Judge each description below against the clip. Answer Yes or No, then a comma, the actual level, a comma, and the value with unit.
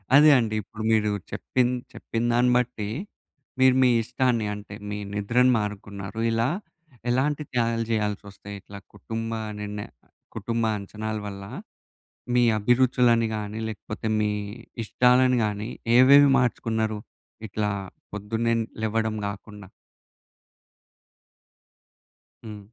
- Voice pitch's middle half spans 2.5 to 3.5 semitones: Yes, average, 2.8 semitones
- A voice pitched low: Yes, low, 110 Hz